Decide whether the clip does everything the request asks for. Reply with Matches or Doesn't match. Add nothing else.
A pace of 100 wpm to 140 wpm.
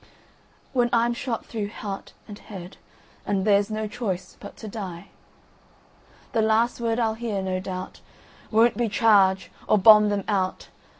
Matches